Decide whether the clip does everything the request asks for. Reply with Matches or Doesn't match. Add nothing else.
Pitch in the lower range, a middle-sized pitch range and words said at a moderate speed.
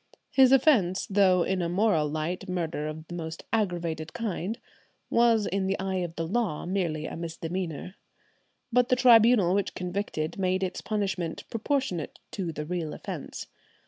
Doesn't match